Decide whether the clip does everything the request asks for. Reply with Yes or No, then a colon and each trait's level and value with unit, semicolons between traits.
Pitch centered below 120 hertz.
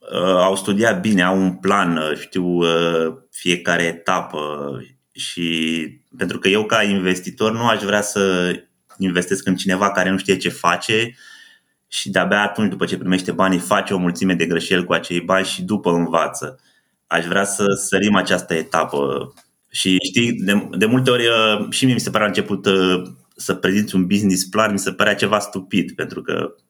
Yes: very low, 95 Hz